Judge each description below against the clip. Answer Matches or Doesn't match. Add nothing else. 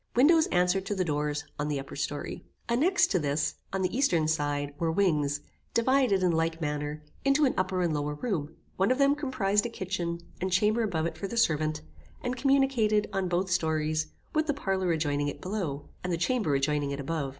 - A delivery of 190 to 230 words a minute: Matches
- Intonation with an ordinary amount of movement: Doesn't match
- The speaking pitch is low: Doesn't match